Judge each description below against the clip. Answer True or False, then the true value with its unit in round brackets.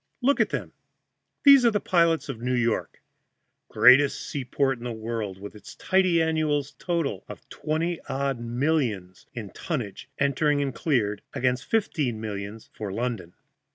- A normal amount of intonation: False (6.0 semitones)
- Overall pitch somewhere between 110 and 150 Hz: True (135 Hz)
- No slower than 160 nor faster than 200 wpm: False (150 wpm)